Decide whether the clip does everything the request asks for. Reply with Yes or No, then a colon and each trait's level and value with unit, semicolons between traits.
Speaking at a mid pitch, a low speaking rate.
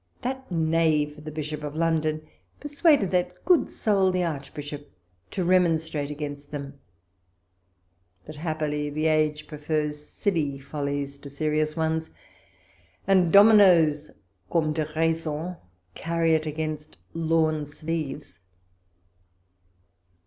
Yes: medium, 155 Hz; slow, 105 wpm